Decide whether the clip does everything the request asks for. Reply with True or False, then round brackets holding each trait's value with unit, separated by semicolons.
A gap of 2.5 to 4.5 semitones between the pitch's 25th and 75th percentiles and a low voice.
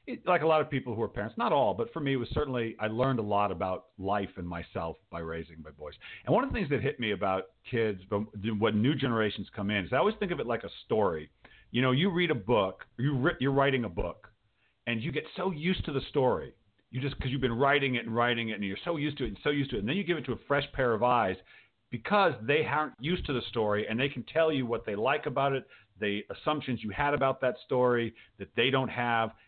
False (5.0 semitones; 125 Hz)